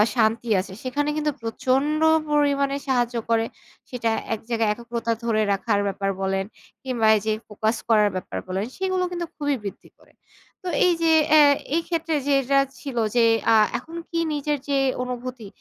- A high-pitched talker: Yes, high, 245 Hz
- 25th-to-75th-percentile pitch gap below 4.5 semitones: No, average, 4.8 semitones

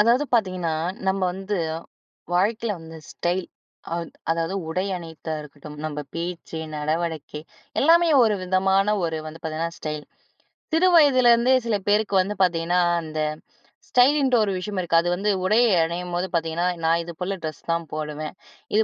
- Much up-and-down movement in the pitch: No, average, 4.4 semitones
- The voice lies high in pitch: No, medium, 180 Hz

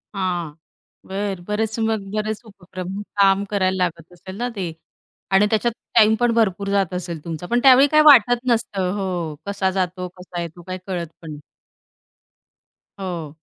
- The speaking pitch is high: Yes, high, 195 Hz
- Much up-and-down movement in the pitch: No, average, 3.2 semitones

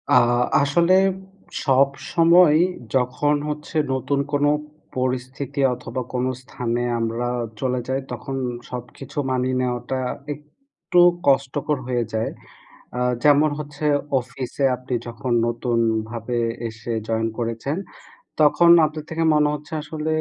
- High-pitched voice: No, low, 130 Hz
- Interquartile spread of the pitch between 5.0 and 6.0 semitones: No, average, 3.4 semitones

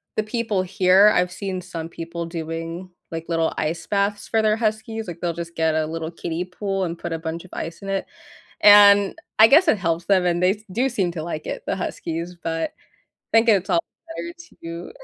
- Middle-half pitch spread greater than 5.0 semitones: No, average, 3.6 semitones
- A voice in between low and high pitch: Yes, medium, 180 Hz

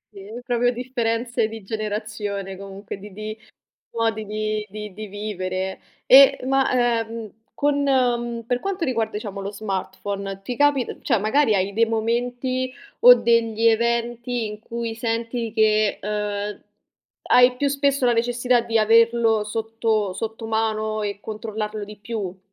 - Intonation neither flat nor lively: No, narrow, 2.2 semitones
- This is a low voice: No, high, 225 Hz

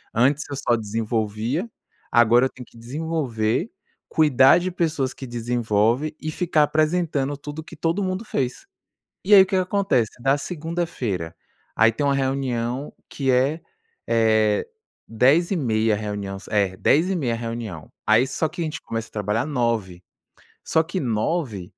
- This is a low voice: Yes, low, 130 Hz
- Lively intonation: Yes, wide, 5.9 semitones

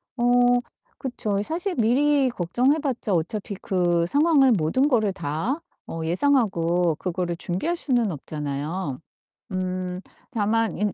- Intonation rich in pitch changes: Yes, wide, 7.0 semitones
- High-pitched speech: Yes, high, 200 Hz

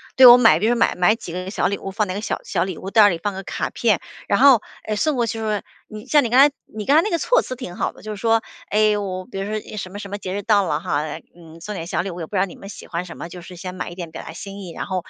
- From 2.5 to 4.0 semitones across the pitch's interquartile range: Yes, average, 3.4 semitones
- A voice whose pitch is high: Yes, high, 200 Hz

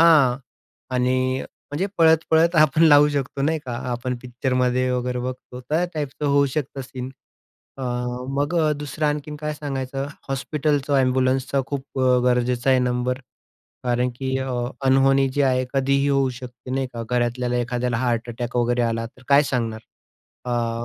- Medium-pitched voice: No, low, 130 Hz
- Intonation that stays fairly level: Yes, narrow, 2.3 semitones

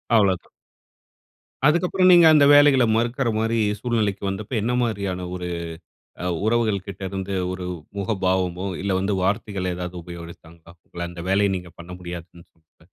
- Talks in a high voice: No, very low, 95 Hz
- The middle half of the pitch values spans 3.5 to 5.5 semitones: Yes, average, 4.2 semitones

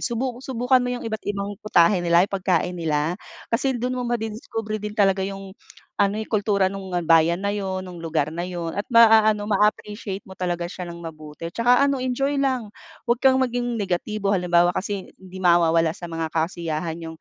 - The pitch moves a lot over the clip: No, average, 4.5 semitones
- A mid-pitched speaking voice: No, high, 195 Hz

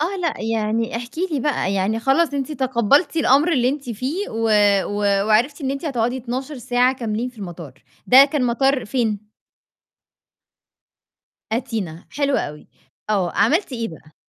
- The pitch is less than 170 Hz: No, high, 245 Hz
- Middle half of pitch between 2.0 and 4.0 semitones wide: No, average, 4.4 semitones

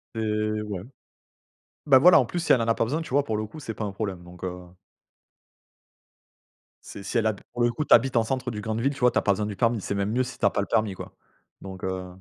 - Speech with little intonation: No, average, 3.7 semitones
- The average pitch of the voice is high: No, low, 110 Hz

